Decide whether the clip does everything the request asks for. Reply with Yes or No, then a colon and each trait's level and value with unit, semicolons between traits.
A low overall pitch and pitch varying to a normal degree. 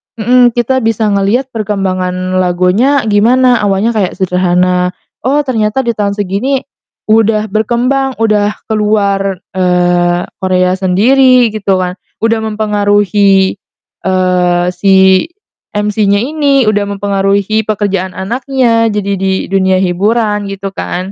No: high, 205 Hz; average, 3.2 semitones